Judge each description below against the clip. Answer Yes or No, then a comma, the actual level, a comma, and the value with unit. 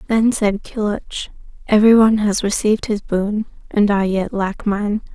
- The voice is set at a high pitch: Yes, high, 210 Hz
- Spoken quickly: No, average, 165 wpm